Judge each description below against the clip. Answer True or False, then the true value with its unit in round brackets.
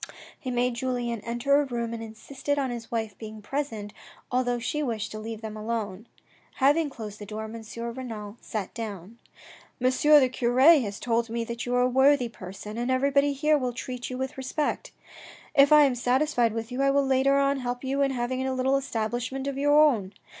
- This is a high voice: True (245 Hz)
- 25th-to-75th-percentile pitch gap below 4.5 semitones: True (3.2 semitones)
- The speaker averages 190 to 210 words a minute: True (205 wpm)